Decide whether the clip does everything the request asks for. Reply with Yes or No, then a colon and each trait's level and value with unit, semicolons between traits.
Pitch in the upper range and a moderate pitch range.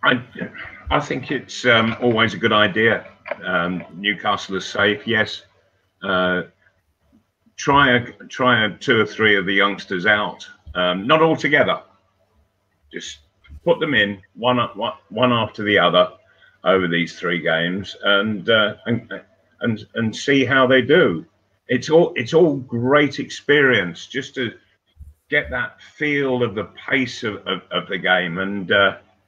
No: low, 105 Hz; average, 4.7 semitones